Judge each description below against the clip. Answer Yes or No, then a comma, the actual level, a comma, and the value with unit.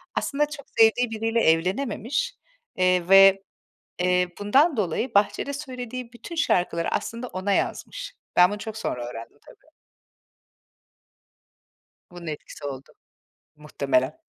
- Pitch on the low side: No, high, 205 Hz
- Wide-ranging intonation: Yes, wide, 6.0 semitones